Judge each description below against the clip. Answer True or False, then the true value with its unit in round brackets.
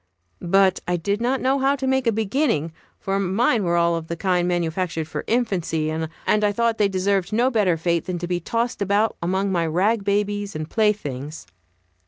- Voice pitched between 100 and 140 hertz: False (195 Hz)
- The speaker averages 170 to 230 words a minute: True (195 wpm)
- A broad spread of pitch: False (4.3 semitones)